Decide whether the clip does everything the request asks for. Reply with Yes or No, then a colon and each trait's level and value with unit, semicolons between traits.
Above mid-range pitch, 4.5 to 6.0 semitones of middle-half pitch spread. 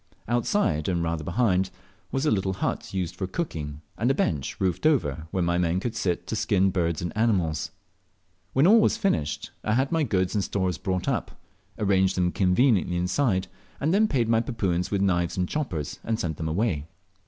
No: very low, 95 Hz; average, 4.9 semitones